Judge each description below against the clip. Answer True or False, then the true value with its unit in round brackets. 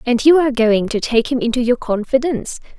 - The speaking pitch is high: True (245 Hz)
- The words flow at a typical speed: False (215 wpm)